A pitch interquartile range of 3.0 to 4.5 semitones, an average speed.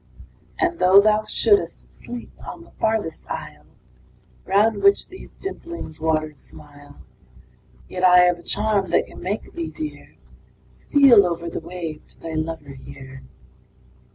No: wide, 5.6 semitones; average, 145 wpm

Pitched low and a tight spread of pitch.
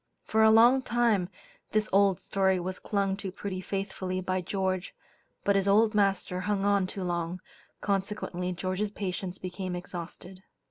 No: high, 190 Hz; narrow, 1.8 semitones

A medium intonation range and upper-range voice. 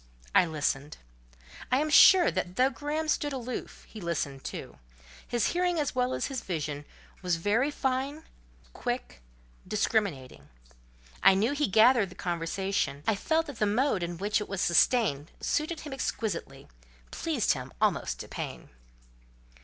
No: wide, 8.3 semitones; high, 210 Hz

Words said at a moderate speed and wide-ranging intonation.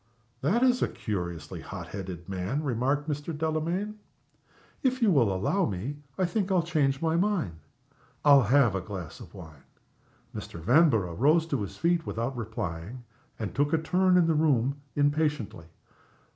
Yes: average, 160 wpm; wide, 8.1 semitones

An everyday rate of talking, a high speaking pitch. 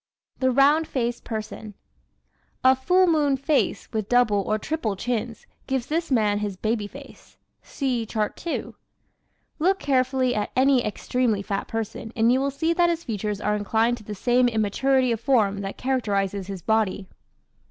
Yes: average, 165 wpm; high, 240 Hz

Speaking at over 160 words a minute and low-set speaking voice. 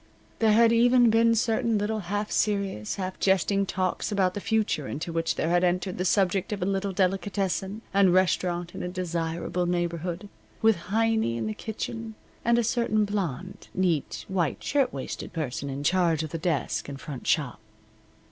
No: average, 170 wpm; medium, 185 Hz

